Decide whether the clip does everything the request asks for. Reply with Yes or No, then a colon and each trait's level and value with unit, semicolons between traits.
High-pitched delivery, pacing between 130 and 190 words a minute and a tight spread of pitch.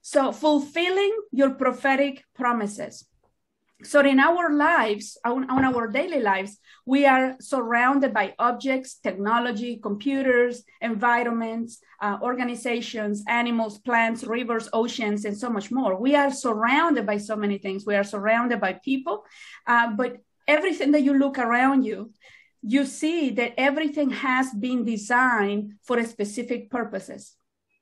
No: high, 245 Hz; slow, 135 wpm; average, 3.3 semitones